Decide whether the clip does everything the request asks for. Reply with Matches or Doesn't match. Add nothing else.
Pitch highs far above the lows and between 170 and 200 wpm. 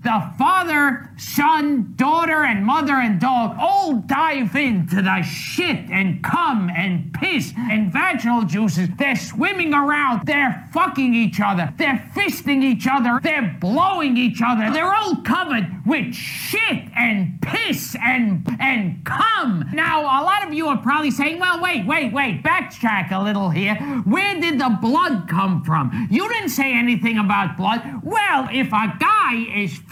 Doesn't match